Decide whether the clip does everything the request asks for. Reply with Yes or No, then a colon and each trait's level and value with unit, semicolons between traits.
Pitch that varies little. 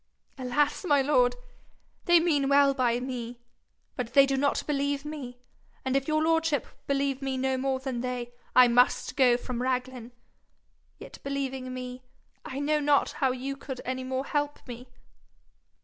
Yes: narrow, 2.1 semitones